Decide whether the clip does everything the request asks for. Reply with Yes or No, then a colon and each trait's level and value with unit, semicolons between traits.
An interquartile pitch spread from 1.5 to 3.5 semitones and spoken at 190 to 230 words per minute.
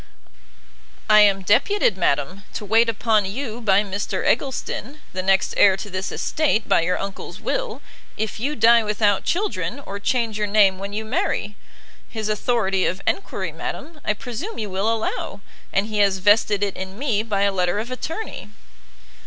No: average, 2.9 semitones; average, 170 wpm